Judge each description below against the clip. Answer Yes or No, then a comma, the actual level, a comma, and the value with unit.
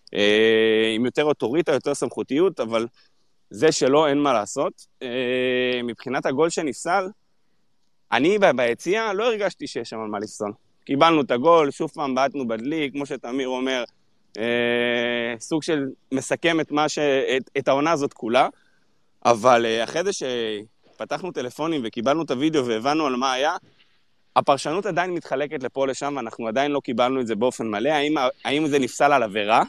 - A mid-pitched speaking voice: No, low, 130 Hz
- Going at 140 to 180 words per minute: Yes, fast, 150 wpm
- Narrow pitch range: No, average, 4.0 semitones